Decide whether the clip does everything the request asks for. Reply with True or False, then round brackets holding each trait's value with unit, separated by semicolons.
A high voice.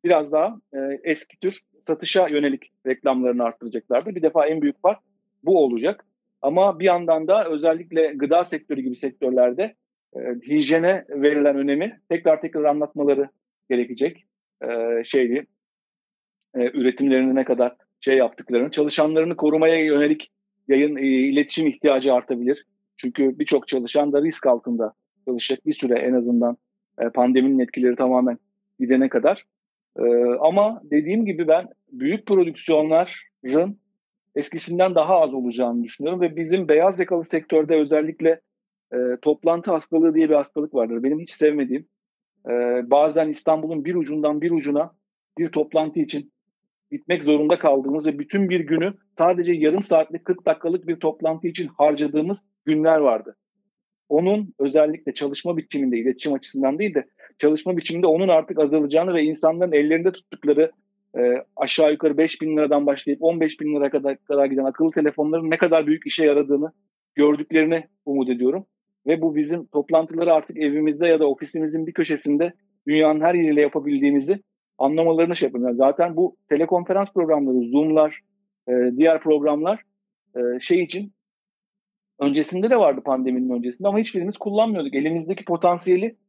False (155 Hz)